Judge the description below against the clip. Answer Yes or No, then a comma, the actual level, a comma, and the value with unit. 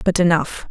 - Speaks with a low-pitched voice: No, medium, 175 Hz